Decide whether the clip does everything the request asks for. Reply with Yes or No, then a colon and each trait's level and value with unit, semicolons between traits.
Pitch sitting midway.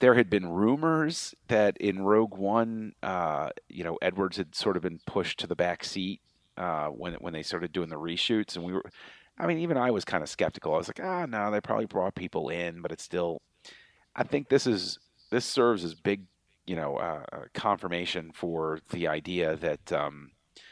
No: very low, 95 Hz